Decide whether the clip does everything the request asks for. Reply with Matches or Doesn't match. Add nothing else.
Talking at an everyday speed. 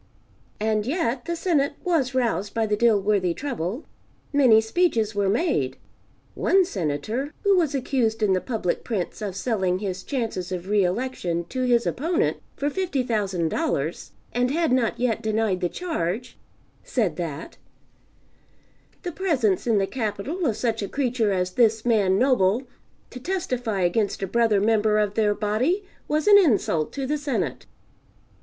Matches